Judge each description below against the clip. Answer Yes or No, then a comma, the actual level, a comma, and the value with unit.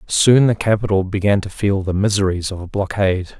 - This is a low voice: Yes, low, 100 Hz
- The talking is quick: No, average, 195 wpm